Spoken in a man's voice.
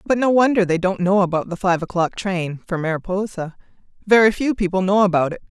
No: female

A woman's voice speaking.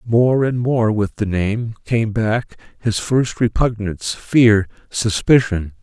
No: male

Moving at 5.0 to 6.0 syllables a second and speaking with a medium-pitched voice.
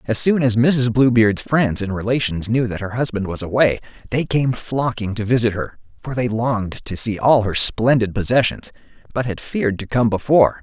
No: 5.1 syllables/s; low, 115 Hz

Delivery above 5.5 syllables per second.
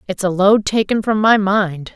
No: 4.5 syllables/s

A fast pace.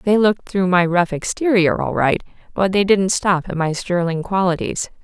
No: average, 190 wpm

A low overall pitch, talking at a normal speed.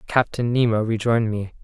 Yes: low, 115 Hz; average, 145 wpm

